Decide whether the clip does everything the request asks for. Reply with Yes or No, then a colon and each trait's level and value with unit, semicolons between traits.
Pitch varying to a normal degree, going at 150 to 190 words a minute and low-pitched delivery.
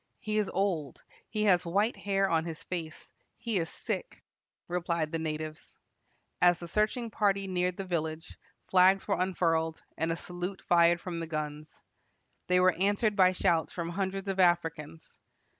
No: average, 3.0 semitones; average, 160 wpm; medium, 180 Hz